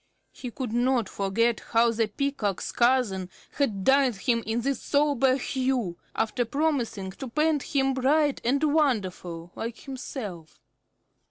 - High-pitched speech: Yes, high, 245 Hz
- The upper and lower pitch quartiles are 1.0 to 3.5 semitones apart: No, average, 4.1 semitones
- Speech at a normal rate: No, slow, 125 wpm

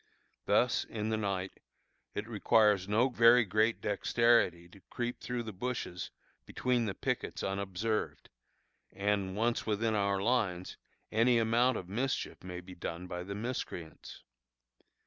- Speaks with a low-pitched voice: Yes, low, 105 Hz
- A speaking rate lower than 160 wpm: Yes, slow, 135 wpm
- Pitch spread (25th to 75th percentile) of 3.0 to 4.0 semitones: Yes, average, 3.7 semitones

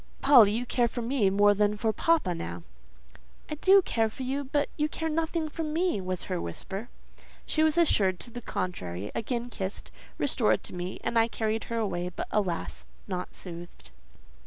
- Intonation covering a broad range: Yes, wide, 7.3 semitones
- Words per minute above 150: Yes, average, 180 wpm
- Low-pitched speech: No, high, 225 Hz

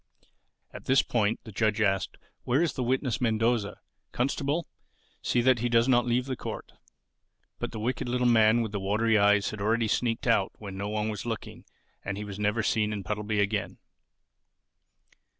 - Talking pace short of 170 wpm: No, average, 180 wpm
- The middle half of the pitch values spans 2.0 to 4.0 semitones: Yes, average, 2.7 semitones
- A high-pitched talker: No, low, 110 Hz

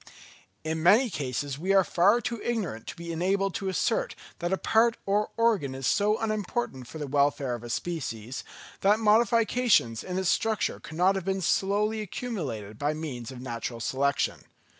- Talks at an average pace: Yes, average, 175 wpm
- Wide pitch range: Yes, wide, 7.4 semitones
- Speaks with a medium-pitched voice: Yes, medium, 180 Hz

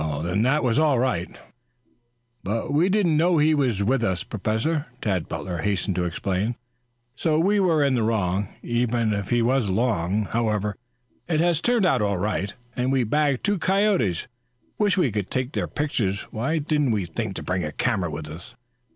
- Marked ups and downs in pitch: Yes, wide, 7.2 semitones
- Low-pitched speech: Yes, low, 120 Hz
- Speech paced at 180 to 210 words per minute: Yes, average, 185 wpm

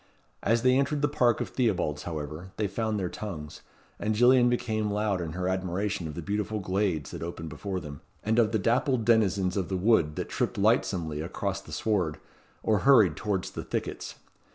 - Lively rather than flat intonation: No, average, 4.3 semitones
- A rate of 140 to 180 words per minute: No, average, 190 wpm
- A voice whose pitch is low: Yes, low, 100 Hz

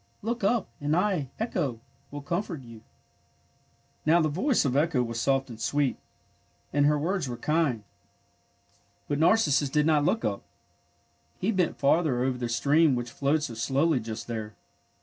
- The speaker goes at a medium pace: Yes, average, 170 wpm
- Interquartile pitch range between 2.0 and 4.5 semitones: No, average, 5.1 semitones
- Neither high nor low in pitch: Yes, medium, 145 Hz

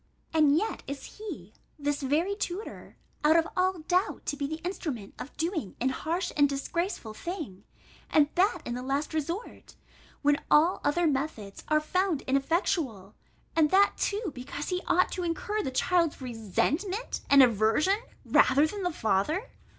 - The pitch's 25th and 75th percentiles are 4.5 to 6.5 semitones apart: Yes, average, 5.0 semitones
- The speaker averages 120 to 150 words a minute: No, average, 160 wpm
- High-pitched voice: Yes, very high, 310 Hz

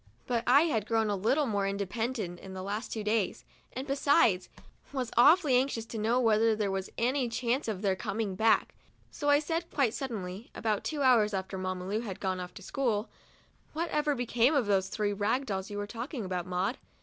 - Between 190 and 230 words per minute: Yes, fast, 205 wpm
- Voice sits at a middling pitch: No, high, 220 Hz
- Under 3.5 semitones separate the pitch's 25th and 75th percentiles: No, average, 4.5 semitones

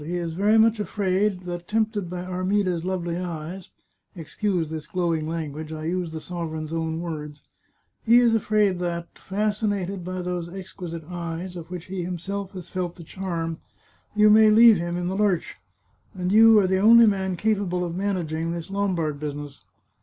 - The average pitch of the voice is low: No, medium, 180 Hz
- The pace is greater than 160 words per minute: Yes, average, 175 wpm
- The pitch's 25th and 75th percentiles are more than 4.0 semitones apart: No, average, 3.1 semitones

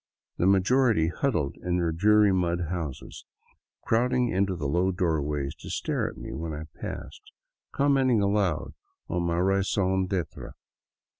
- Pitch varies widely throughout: No, average, 3.8 semitones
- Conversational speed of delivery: Yes, average, 145 wpm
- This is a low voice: Yes, very low, 95 Hz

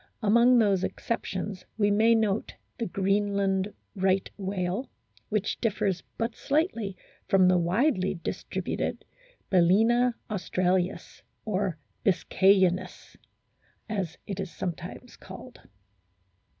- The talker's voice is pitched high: Yes, high, 195 Hz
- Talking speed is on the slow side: Yes, slow, 100 wpm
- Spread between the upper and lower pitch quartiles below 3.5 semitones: Yes, average, 2.7 semitones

